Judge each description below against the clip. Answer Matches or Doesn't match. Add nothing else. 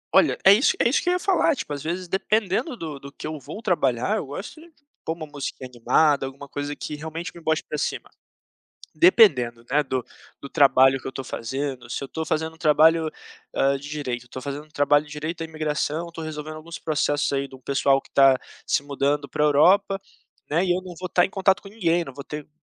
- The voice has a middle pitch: Matches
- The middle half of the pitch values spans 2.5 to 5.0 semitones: Matches